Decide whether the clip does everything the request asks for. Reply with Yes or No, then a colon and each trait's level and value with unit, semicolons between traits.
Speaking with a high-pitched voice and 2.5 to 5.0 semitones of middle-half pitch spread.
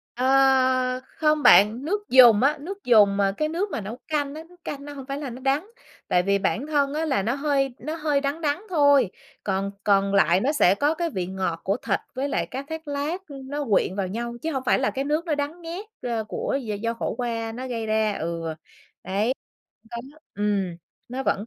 No: very high, 265 Hz; wide, 5.4 semitones